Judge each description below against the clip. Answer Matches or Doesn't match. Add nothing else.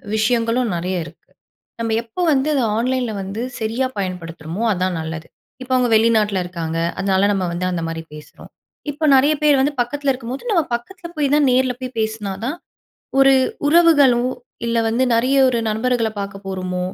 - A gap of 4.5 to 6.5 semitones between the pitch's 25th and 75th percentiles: Matches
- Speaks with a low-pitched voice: Doesn't match